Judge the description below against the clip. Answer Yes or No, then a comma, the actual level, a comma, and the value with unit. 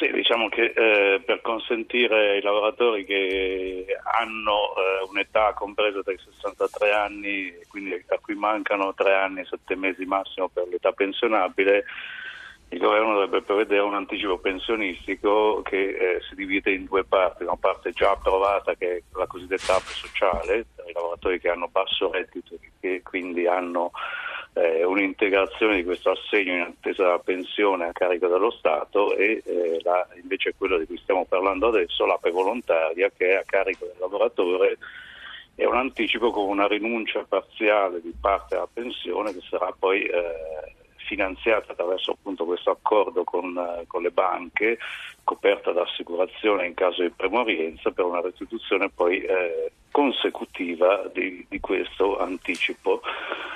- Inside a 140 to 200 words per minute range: Yes, average, 155 wpm